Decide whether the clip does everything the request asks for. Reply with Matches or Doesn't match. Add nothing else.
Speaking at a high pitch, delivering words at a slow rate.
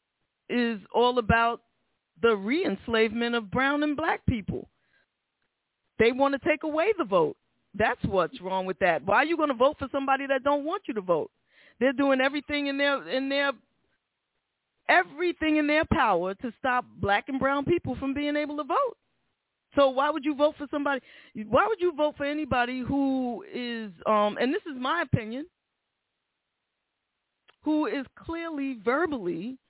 Doesn't match